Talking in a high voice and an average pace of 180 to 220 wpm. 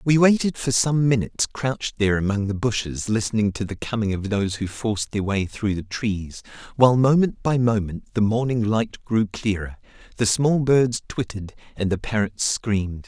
No: low, 110 Hz; average, 185 wpm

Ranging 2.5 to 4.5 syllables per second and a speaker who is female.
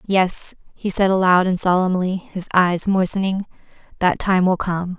Yes: 4.4 syllables/s; female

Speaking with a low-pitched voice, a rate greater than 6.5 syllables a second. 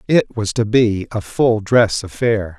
No: low, 110 Hz; 3.8 syllables/s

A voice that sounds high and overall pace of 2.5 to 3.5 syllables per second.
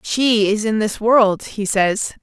Yes: high, 215 Hz; 3.4 syllables/s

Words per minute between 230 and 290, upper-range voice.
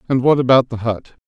No: fast, 235 wpm; low, 125 Hz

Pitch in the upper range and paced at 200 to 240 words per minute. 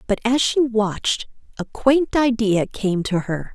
No: high, 225 Hz; average, 170 wpm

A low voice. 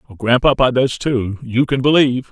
Yes: low, 125 Hz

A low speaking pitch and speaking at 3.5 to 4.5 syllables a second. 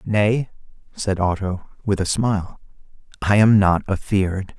Yes: low, 100 Hz; 4.3 syllables/s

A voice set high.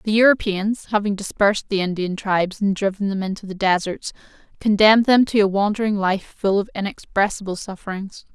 Yes: high, 200 Hz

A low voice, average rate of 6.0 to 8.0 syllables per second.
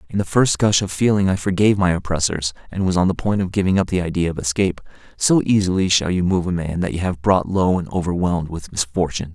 Yes: very low, 90 Hz; 6.4 syllables/s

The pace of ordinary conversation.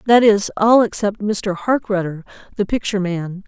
Yes: average, 155 wpm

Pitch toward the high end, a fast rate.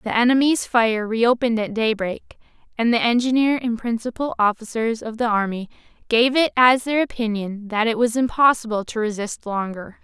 No: high, 230 Hz; average, 160 wpm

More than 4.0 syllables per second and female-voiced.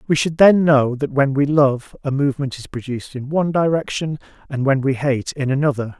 No: 5.5 syllables/s; male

